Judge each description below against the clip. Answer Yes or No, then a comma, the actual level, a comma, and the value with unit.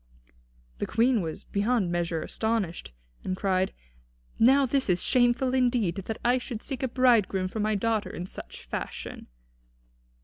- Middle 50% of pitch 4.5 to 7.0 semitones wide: Yes, average, 5.0 semitones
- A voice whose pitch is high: Yes, high, 225 Hz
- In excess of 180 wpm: No, average, 145 wpm